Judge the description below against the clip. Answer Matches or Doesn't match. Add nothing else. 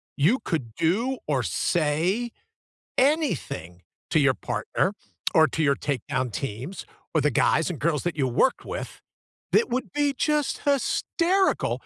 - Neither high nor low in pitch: Matches